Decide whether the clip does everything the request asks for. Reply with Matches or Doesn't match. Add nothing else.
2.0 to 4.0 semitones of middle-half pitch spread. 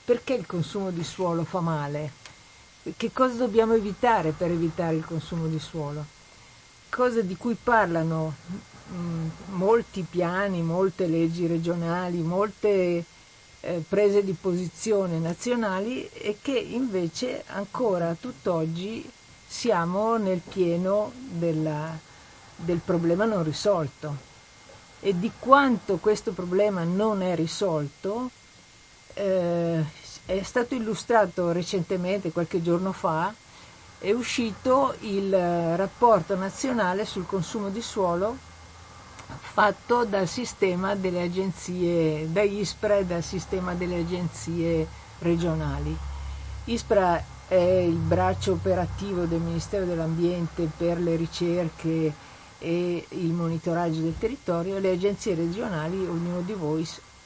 Matches